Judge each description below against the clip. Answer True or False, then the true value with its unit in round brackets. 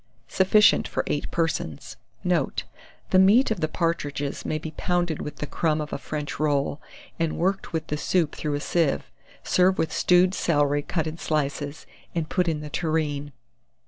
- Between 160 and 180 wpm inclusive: True (175 wpm)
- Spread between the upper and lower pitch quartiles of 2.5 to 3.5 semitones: True (3.0 semitones)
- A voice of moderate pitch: True (155 Hz)